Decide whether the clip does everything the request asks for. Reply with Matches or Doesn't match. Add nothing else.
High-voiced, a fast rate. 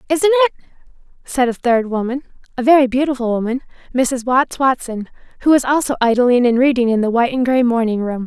Doesn't match